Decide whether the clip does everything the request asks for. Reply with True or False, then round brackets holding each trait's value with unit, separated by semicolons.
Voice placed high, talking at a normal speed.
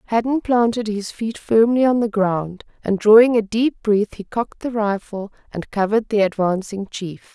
True (215 Hz; 180 wpm)